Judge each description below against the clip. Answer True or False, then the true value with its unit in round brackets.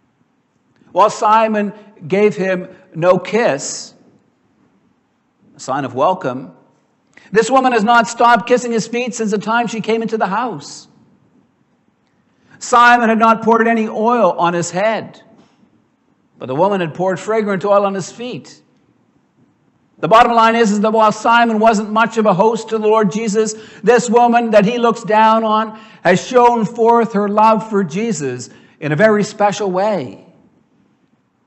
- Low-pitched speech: False (220 Hz)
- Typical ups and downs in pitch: False (2.3 semitones)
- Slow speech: False (155 wpm)